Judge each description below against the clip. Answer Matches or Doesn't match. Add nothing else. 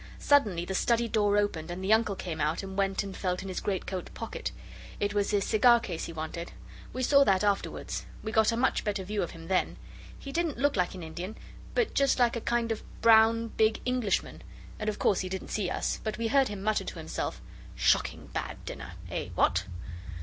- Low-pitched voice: Doesn't match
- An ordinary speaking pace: Doesn't match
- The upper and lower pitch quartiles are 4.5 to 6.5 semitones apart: Doesn't match